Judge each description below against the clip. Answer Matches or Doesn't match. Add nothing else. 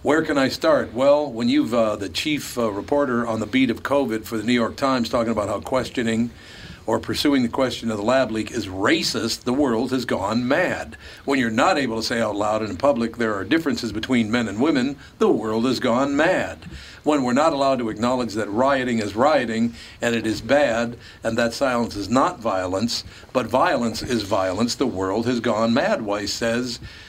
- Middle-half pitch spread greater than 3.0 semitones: Doesn't match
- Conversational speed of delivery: Doesn't match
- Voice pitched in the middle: Doesn't match